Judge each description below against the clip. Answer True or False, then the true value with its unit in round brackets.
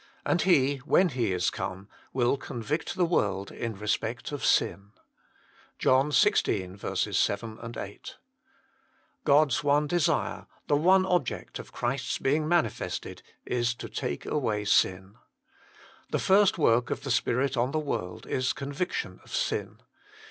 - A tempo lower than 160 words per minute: True (140 wpm)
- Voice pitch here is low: True (130 Hz)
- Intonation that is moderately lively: False (5.9 semitones)